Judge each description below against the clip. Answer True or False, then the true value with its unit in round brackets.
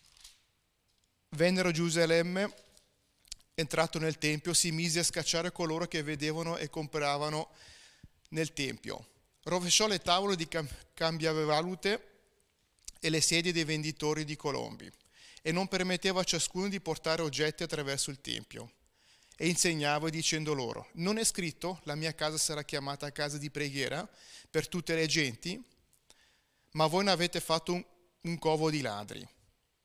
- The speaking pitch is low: False (160 Hz)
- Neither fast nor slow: True (140 wpm)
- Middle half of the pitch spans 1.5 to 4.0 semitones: True (2.4 semitones)